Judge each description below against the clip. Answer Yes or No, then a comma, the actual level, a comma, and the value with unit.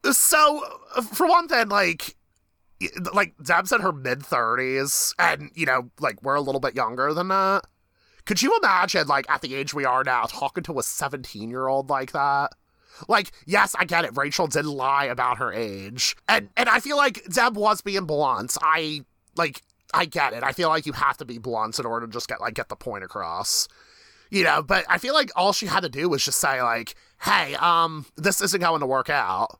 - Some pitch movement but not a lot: No, wide, 7.1 semitones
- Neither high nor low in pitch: Yes, medium, 145 Hz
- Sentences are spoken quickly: Yes, fast, 215 wpm